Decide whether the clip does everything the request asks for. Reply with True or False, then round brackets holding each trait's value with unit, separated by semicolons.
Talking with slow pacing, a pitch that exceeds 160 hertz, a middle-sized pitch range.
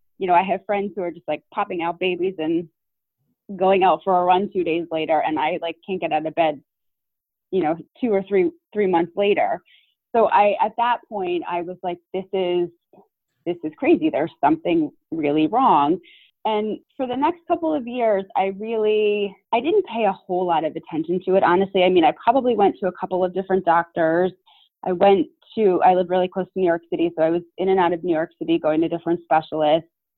False (220 wpm; 185 Hz; 4.0 semitones)